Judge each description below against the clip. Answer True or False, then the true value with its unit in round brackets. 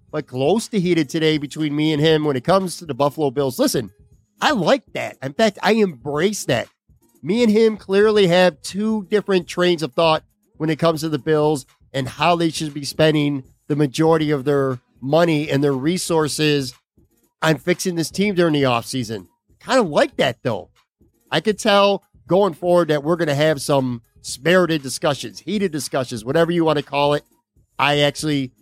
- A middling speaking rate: True (190 wpm)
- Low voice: False (155 Hz)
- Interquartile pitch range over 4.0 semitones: False (3.6 semitones)